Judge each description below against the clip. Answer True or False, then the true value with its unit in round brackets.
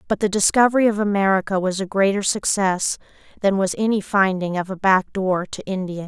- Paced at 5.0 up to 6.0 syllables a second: True (5.6 syllables/s)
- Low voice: False (195 Hz)